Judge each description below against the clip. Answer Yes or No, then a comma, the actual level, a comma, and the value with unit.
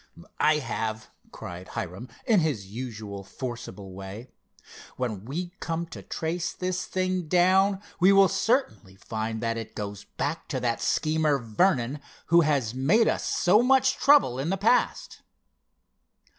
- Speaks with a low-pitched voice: No, medium, 145 Hz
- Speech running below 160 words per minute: Yes, average, 145 wpm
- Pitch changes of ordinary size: No, wide, 8.6 semitones